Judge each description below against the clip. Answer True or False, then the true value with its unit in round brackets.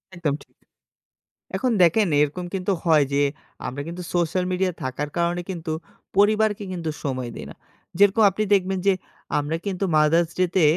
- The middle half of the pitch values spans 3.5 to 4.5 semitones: True (3.9 semitones)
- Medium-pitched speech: True (175 Hz)